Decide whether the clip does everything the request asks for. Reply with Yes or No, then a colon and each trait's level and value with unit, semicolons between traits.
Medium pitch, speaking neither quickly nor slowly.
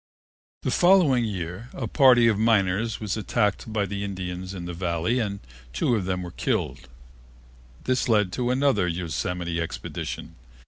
No: low, 100 Hz; average, 150 wpm